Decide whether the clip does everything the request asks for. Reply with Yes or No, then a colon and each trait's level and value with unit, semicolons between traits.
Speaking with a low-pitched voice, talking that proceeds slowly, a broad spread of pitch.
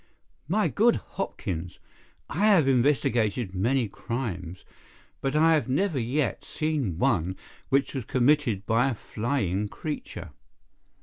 Yes: low, 125 Hz; slow, 120 wpm; wide, 6.3 semitones